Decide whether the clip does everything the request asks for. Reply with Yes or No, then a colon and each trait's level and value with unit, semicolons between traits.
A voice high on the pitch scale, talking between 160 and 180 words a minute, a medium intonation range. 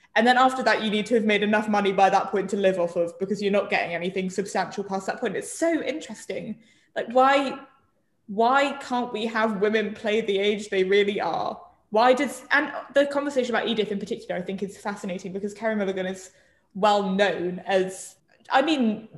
No: high, 210 Hz; fast, 205 wpm; average, 4.0 semitones